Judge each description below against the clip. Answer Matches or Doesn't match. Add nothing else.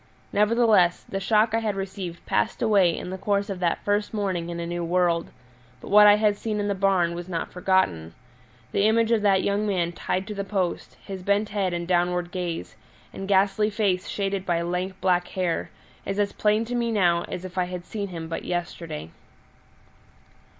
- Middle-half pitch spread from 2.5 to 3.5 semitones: Matches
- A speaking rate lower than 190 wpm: Doesn't match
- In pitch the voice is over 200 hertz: Doesn't match